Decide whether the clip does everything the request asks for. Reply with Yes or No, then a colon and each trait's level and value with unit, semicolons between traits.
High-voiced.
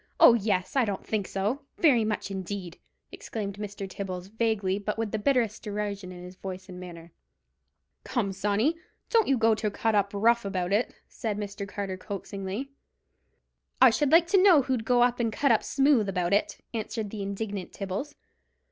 Yes: high, 210 Hz